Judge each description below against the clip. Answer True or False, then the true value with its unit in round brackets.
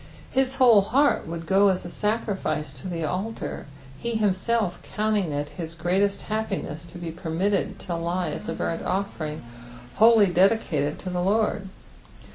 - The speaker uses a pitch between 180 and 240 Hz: True (190 Hz)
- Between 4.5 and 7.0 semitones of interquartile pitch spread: False (4.1 semitones)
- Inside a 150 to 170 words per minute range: True (155 wpm)